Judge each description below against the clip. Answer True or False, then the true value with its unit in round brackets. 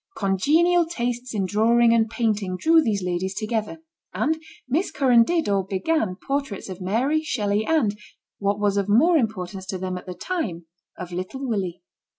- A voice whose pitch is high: True (220 Hz)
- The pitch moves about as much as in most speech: False (6.4 semitones)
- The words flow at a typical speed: True (165 wpm)